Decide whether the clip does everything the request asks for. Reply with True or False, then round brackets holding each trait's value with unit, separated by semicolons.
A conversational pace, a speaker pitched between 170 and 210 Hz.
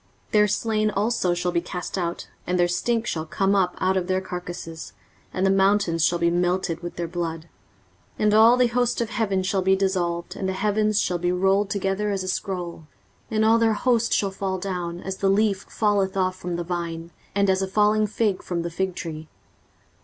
False (215 wpm; 190 Hz)